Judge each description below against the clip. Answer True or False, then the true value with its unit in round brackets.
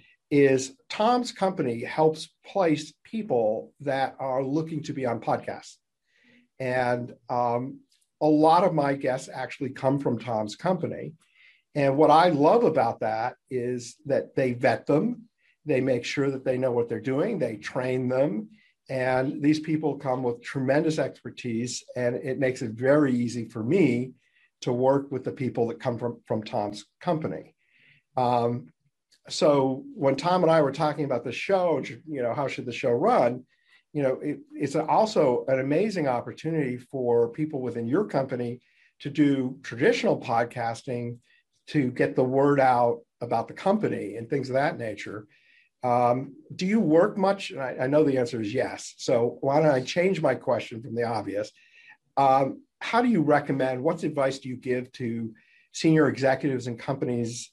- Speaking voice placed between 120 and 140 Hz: True (135 Hz)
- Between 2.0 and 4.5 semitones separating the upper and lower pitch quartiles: True (3.8 semitones)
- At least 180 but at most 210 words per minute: False (170 wpm)